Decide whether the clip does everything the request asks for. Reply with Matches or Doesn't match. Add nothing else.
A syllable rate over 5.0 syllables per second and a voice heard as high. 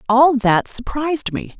Doesn't match